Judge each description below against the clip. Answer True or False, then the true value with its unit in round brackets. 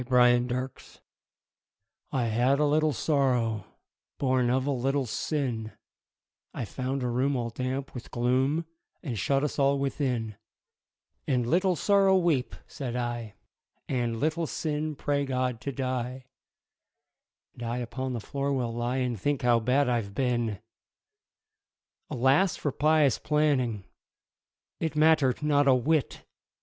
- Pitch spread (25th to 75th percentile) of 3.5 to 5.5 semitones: False (2.9 semitones)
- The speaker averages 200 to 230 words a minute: False (135 wpm)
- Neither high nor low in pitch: False (130 Hz)